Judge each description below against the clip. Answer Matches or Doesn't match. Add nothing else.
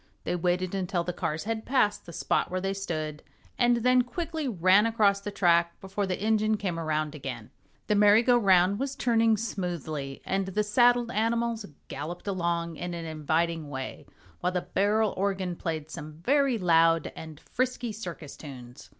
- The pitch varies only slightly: Doesn't match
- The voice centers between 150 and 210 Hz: Matches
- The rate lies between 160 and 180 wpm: Matches